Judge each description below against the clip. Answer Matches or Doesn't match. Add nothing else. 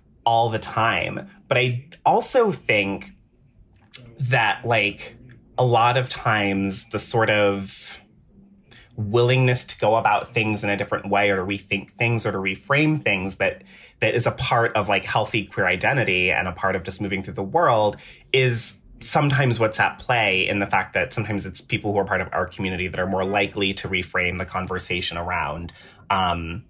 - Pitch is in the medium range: Doesn't match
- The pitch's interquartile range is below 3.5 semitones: Doesn't match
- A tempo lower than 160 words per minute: Doesn't match